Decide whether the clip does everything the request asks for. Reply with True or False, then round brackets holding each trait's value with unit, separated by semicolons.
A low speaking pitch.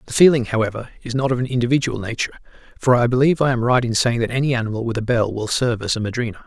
True (120 Hz)